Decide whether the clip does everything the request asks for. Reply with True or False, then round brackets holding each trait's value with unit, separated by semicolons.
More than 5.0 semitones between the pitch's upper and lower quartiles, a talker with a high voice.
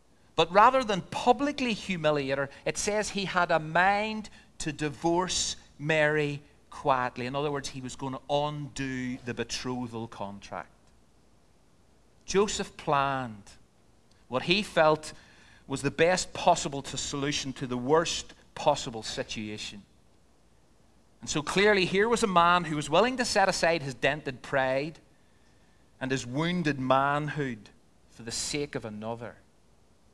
False (5.6 semitones; 140 Hz)